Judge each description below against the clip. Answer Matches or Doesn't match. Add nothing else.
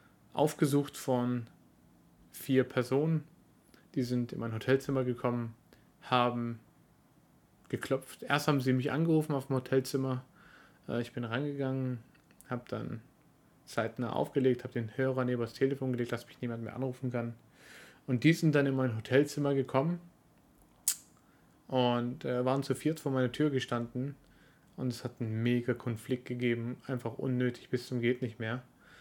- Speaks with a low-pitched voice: Matches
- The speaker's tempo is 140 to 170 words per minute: Matches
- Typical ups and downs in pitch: Doesn't match